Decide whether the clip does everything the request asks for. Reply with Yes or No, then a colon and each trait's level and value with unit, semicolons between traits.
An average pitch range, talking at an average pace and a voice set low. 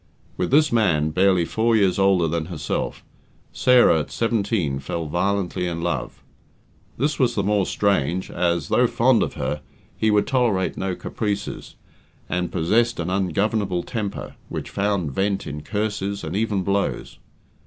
Yes: average, 3.5 semitones; average, 150 wpm; low, 100 Hz